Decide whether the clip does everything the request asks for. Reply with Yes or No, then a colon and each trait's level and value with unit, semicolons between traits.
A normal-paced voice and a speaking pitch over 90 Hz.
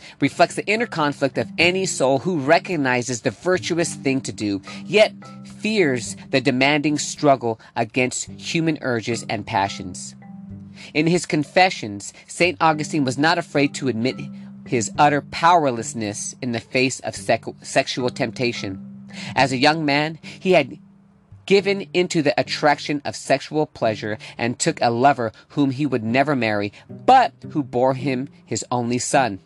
Yes: average, 150 wpm; low, 135 Hz